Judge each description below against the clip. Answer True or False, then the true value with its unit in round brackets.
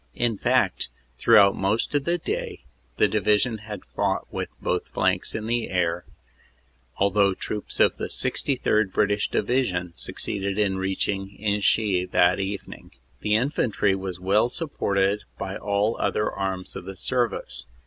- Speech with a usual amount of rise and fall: False (2.1 semitones)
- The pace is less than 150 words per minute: True (140 wpm)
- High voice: False (100 Hz)